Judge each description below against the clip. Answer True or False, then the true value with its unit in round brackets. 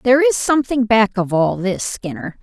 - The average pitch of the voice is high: True (210 Hz)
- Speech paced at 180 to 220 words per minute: True (200 wpm)